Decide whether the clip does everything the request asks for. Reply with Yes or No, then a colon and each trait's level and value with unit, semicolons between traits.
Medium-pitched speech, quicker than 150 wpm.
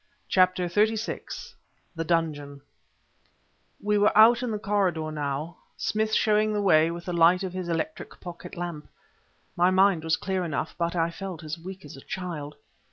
Yes: medium, 175 Hz; average, 165 wpm